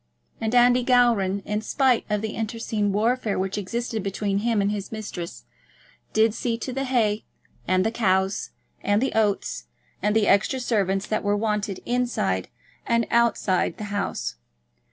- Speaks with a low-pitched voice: No, high, 210 Hz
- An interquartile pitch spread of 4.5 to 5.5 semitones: No, average, 2.8 semitones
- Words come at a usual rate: Yes, average, 160 wpm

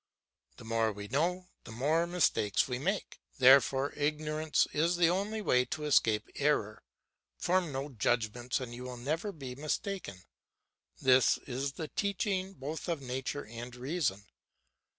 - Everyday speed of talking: Yes, average, 145 wpm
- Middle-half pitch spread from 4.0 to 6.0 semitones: Yes, average, 5.3 semitones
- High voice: No, medium, 140 Hz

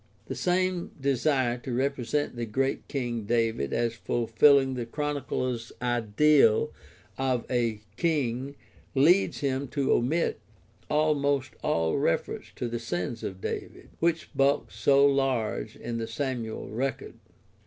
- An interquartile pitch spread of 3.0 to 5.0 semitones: Yes, average, 3.3 semitones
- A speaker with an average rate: No, slow, 125 wpm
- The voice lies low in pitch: Yes, low, 130 Hz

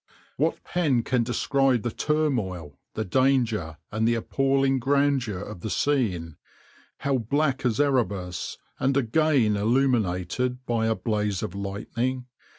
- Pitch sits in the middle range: No, low, 120 Hz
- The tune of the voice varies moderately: Yes, average, 4.7 semitones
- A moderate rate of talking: No, slow, 130 wpm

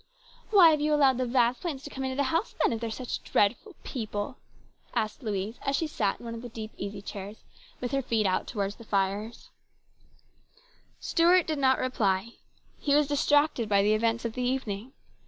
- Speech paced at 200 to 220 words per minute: Yes, fast, 205 wpm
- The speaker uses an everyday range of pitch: Yes, average, 4.7 semitones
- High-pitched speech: Yes, high, 240 Hz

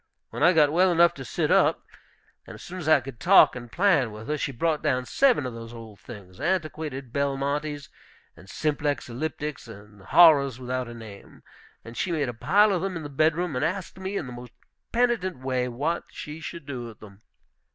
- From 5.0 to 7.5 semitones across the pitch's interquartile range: Yes, wide, 5.5 semitones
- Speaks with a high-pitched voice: No, medium, 140 Hz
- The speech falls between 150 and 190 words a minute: No, fast, 205 wpm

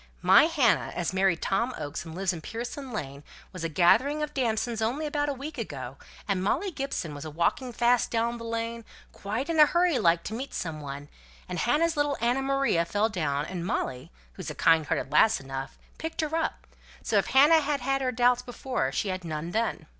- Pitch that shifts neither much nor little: No, wide, 8.3 semitones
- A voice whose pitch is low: No, high, 225 Hz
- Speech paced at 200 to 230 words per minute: Yes, fast, 205 wpm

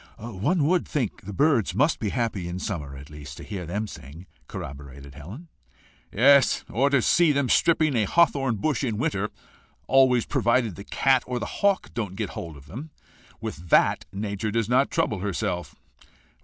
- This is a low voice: Yes, low, 110 Hz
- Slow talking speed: No, average, 175 wpm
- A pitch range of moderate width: No, wide, 6.9 semitones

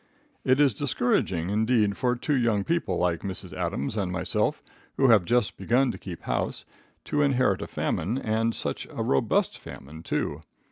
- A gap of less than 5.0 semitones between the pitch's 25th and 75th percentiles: No, wide, 5.6 semitones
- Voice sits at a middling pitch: No, low, 110 Hz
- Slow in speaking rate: No, average, 170 wpm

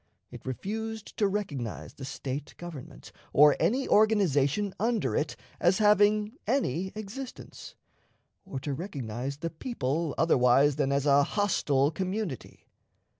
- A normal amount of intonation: No, wide, 7.1 semitones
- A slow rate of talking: Yes, slow, 125 wpm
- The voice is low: No, medium, 165 Hz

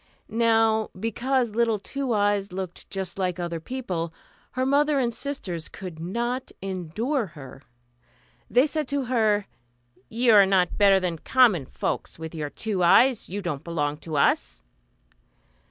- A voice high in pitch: Yes, high, 205 Hz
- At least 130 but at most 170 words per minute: Yes, average, 145 wpm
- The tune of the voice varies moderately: No, wide, 5.8 semitones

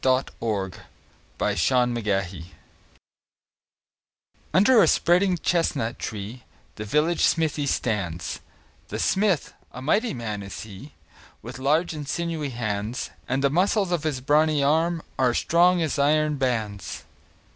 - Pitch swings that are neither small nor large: No, wide, 6.6 semitones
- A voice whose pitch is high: No, medium, 140 Hz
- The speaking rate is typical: No, slow, 125 wpm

